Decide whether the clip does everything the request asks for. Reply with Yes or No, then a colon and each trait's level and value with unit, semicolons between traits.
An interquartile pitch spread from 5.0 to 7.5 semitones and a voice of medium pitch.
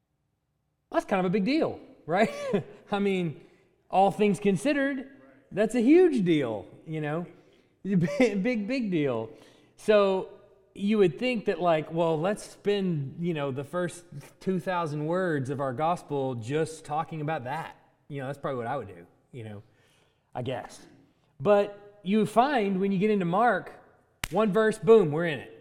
Yes: wide, 5.6 semitones; medium, 180 Hz